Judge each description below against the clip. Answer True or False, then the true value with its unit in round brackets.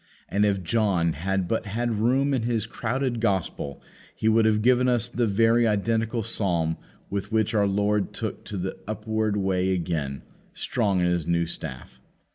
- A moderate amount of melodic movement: True (3.6 semitones)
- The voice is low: True (105 Hz)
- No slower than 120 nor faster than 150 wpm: False (170 wpm)